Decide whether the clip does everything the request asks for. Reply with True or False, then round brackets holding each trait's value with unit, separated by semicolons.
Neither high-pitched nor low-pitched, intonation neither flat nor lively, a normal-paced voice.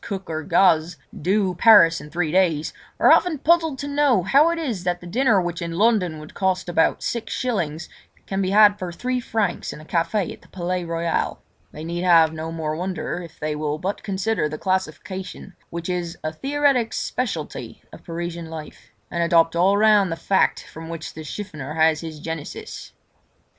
True (175 Hz; 4.1 semitones; 190 wpm)